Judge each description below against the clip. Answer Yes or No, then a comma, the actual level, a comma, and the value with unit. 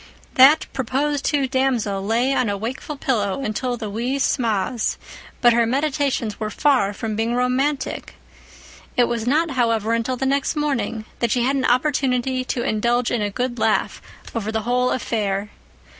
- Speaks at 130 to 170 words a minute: Yes, average, 165 wpm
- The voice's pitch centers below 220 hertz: No, high, 245 Hz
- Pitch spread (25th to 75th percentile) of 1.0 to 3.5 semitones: Yes, average, 3.2 semitones